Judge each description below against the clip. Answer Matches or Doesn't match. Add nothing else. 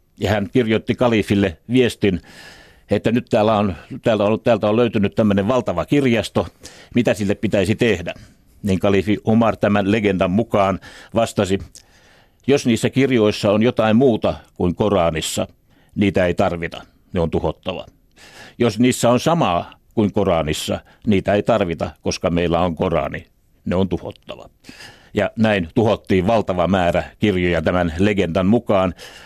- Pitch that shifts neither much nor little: Matches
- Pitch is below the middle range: Matches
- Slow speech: Doesn't match